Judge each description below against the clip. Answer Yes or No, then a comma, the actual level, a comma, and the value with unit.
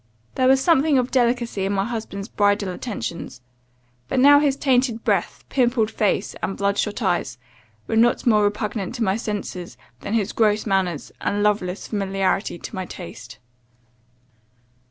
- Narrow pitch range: No, average, 3.7 semitones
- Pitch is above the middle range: Yes, high, 210 Hz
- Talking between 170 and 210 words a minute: No, average, 155 wpm